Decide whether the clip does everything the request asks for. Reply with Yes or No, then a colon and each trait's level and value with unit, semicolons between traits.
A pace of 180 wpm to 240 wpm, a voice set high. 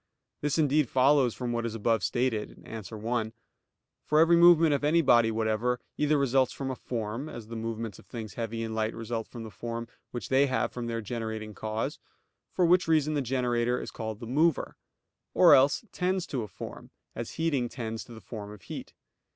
No: average, 200 wpm; low, 120 Hz